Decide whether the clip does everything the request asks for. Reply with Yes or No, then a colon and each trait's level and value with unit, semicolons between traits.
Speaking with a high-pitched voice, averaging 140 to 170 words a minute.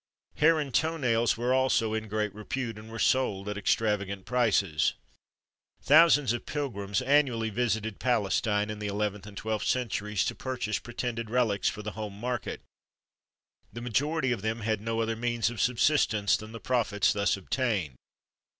No: low, 110 Hz; average, 160 wpm